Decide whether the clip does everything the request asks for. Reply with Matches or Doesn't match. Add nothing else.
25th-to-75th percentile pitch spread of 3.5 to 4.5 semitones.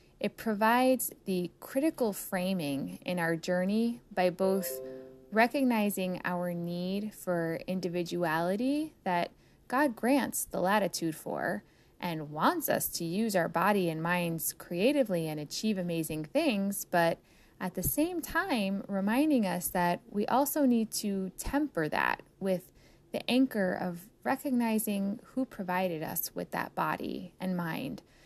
Doesn't match